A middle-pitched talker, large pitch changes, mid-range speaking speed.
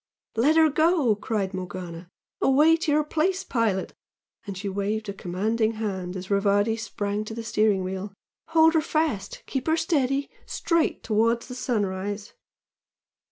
No: high, 220 Hz; wide, 6.7 semitones; average, 155 wpm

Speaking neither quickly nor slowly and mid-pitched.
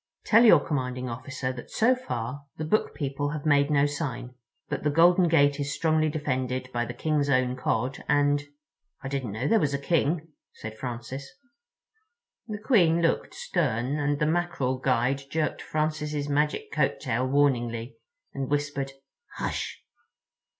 Yes: average, 150 wpm; medium, 145 Hz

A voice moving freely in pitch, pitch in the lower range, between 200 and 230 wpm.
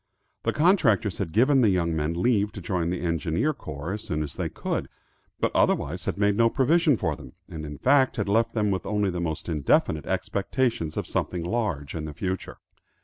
Yes: wide, 6.0 semitones; very low, 95 Hz; fast, 205 wpm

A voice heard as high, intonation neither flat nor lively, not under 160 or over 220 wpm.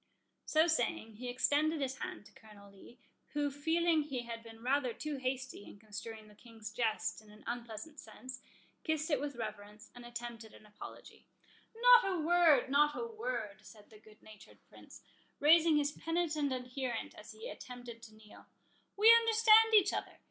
No: very high, 250 Hz; wide, 5.9 semitones; average, 170 wpm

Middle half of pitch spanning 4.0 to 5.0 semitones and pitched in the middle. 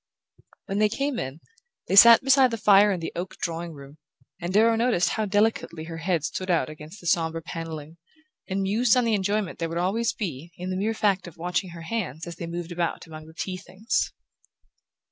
Yes: average, 4.3 semitones; medium, 180 Hz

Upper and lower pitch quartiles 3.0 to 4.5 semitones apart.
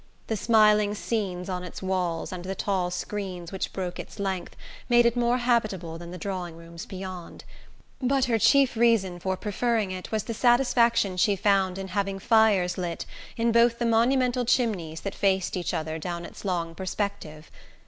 Yes: average, 4.2 semitones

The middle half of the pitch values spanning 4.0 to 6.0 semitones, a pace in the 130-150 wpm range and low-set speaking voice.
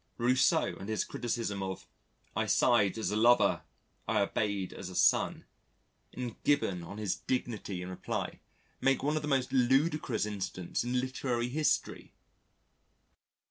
Yes: average, 4.4 semitones; average, 140 wpm; low, 120 Hz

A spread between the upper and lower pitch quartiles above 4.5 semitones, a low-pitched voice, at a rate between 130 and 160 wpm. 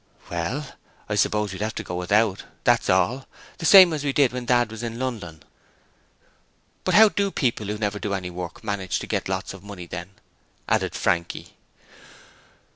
No: wide, 5.4 semitones; low, 105 Hz; average, 185 wpm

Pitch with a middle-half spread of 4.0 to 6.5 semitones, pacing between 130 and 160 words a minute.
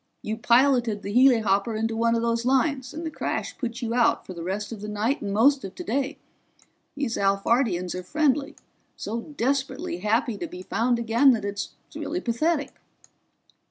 No: average, 4.3 semitones; average, 175 wpm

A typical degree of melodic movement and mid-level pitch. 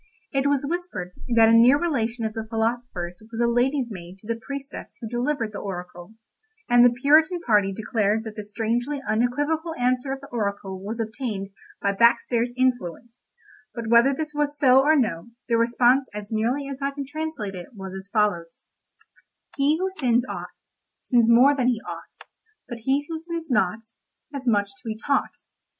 No: average, 4.4 semitones; high, 240 Hz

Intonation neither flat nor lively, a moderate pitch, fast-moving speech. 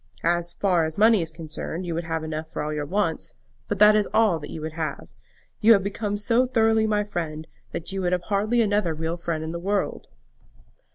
Yes: average, 4.4 semitones; medium, 175 Hz; fast, 215 wpm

